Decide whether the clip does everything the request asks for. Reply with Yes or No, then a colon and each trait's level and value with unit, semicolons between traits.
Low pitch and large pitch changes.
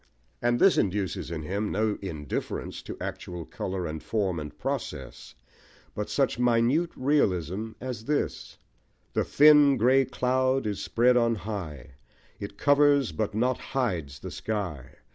Yes: low, 110 Hz; wide, 6.0 semitones